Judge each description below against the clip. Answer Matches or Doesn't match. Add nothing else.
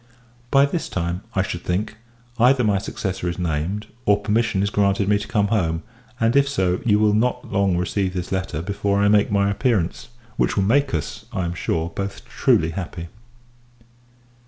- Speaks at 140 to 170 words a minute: Doesn't match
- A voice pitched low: Matches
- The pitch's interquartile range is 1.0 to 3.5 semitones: Matches